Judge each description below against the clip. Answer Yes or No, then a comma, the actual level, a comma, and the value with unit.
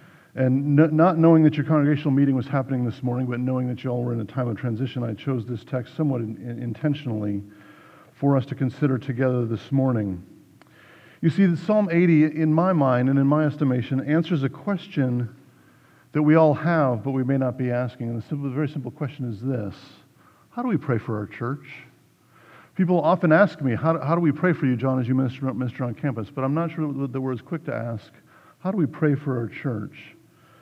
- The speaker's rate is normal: No, fast, 225 wpm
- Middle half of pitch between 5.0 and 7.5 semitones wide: No, average, 3.8 semitones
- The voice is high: No, low, 135 Hz